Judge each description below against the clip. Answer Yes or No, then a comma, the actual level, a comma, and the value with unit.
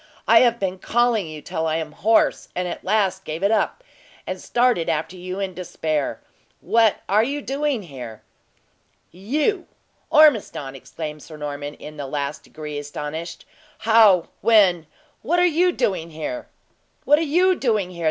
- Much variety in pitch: Yes, wide, 7.2 semitones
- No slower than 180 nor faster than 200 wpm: No, average, 160 wpm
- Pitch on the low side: No, medium, 185 Hz